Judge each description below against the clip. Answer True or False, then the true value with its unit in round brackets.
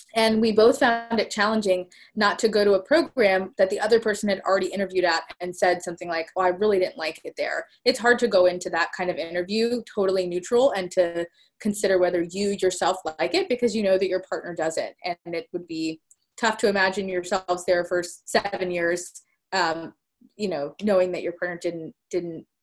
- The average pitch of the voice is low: False (190 Hz)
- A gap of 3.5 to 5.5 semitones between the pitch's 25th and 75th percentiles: False (3.1 semitones)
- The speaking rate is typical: False (210 wpm)